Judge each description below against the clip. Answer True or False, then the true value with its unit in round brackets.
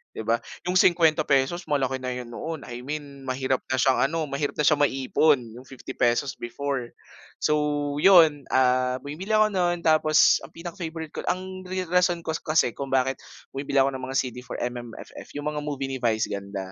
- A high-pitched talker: False (140 Hz)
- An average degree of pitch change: True (3.8 semitones)